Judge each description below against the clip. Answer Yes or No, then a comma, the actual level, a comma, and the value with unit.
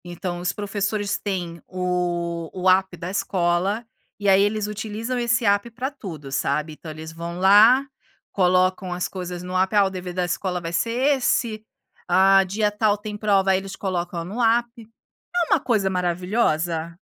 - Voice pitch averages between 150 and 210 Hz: Yes, high, 190 Hz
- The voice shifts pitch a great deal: No, average, 3.1 semitones